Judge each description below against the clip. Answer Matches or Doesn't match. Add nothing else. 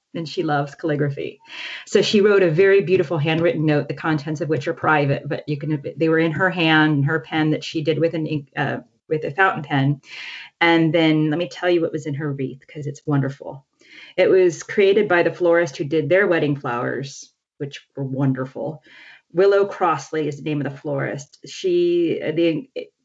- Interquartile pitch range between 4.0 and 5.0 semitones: Doesn't match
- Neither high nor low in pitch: Matches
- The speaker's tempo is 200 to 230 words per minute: Matches